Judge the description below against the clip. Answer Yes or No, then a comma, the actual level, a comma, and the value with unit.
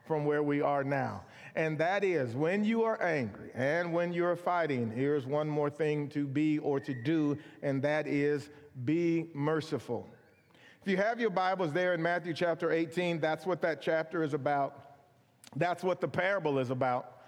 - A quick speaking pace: No, average, 180 wpm